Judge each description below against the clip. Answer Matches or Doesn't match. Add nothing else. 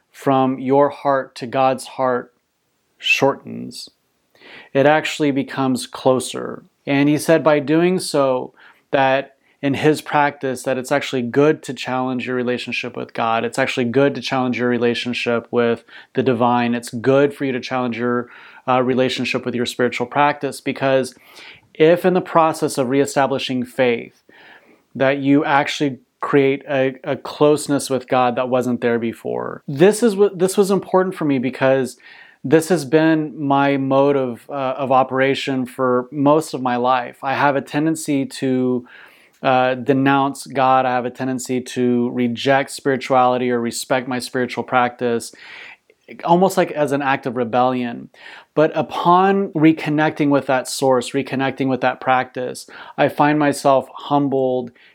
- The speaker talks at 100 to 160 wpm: Matches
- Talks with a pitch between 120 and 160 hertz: Matches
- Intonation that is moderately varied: Doesn't match